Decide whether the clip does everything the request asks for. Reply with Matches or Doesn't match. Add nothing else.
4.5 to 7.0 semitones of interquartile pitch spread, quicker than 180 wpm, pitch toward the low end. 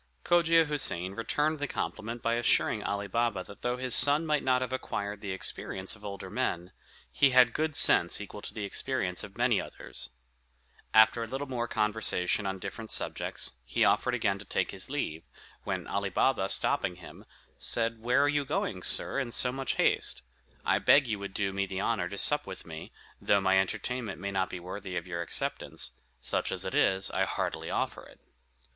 Matches